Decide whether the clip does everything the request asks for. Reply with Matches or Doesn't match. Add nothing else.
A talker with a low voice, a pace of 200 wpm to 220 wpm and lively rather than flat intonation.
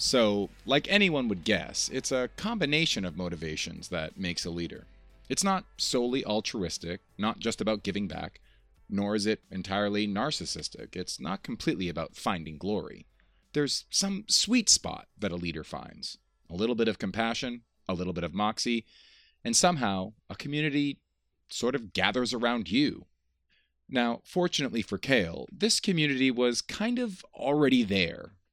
Doesn't match